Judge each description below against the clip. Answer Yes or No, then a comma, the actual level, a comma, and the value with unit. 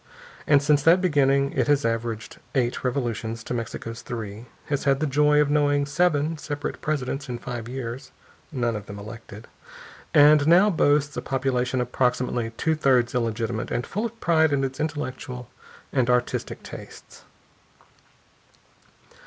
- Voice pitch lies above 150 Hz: No, low, 135 Hz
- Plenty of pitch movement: No, average, 3.6 semitones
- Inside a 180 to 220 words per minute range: No, average, 145 wpm